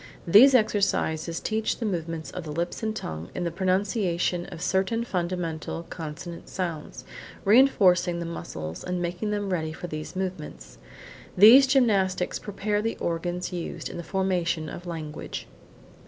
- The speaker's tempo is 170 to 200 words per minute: No, average, 145 wpm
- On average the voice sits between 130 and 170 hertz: No, medium, 180 Hz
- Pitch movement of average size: Yes, average, 3.3 semitones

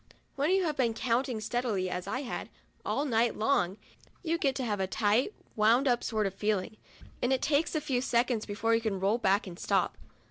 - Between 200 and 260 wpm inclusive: Yes, fast, 205 wpm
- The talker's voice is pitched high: Yes, high, 230 Hz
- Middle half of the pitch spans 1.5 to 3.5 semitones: No, average, 4.2 semitones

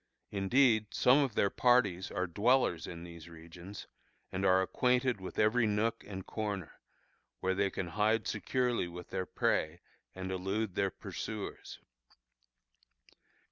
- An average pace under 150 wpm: Yes, slow, 135 wpm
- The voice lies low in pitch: Yes, low, 100 Hz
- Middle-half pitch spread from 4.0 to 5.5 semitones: No, average, 3.6 semitones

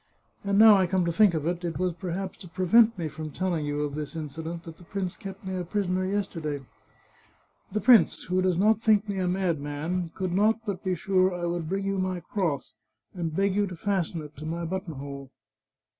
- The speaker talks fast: Yes, fast, 220 wpm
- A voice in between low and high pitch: Yes, medium, 180 Hz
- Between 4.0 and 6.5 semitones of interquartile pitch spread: No, average, 3.0 semitones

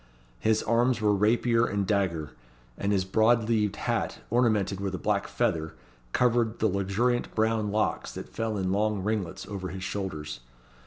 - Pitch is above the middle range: No, low, 105 Hz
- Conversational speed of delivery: Yes, average, 160 wpm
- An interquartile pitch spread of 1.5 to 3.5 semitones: Yes, average, 2.7 semitones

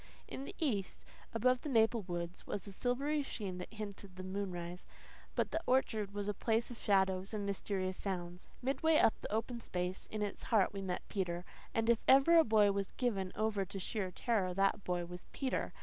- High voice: Yes, high, 200 Hz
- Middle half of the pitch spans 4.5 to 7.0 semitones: No, average, 3.8 semitones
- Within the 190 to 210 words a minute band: Yes, average, 195 wpm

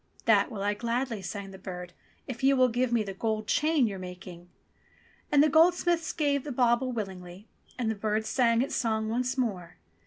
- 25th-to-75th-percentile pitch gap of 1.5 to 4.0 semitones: No, average, 4.5 semitones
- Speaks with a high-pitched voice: Yes, high, 230 Hz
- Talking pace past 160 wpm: Yes, average, 190 wpm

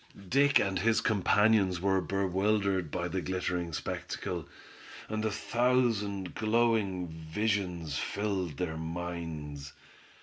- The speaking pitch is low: Yes, very low, 95 Hz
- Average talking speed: No, slow, 105 wpm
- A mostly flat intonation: No, average, 3.7 semitones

